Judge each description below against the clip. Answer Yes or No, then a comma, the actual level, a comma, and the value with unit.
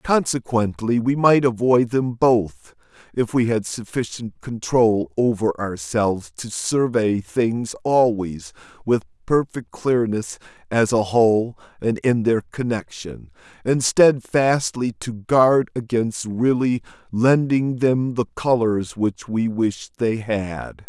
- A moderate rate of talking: No, slow, 120 wpm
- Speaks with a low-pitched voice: Yes, low, 115 Hz